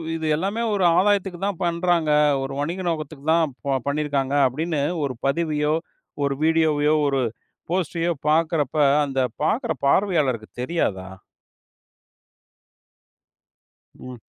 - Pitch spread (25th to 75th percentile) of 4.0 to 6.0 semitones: No, average, 3.6 semitones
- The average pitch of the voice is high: No, medium, 155 Hz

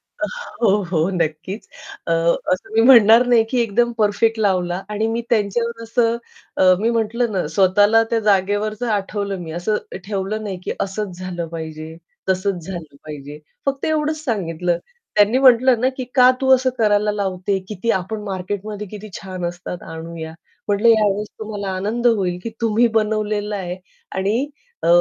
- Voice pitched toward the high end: Yes, high, 205 Hz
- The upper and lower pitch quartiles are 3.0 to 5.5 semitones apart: Yes, average, 3.7 semitones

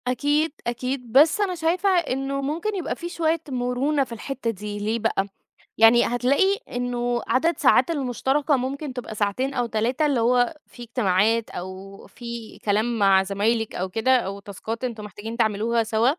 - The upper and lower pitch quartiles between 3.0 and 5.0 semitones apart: Yes, average, 4.0 semitones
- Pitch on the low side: No, high, 245 Hz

